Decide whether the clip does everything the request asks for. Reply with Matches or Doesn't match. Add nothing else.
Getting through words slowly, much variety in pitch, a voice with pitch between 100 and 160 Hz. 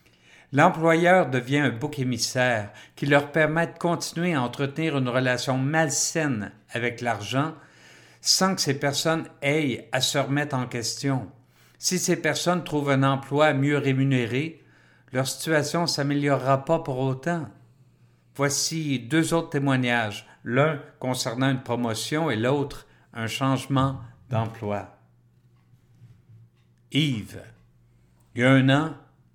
Doesn't match